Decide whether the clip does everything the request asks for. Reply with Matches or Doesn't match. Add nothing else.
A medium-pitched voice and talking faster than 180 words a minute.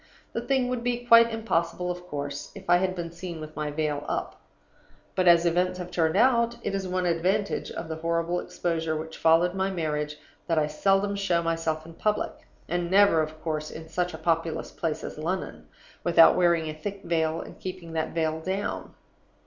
Matches